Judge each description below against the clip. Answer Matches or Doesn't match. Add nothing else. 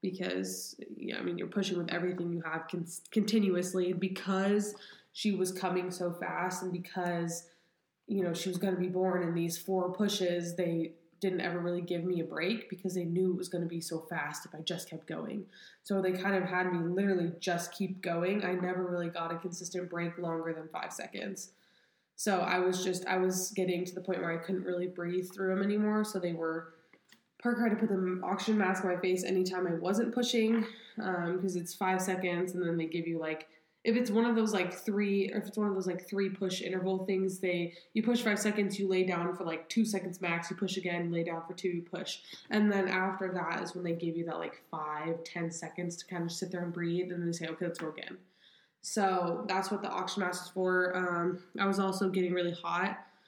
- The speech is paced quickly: Matches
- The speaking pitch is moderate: Matches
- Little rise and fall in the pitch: Matches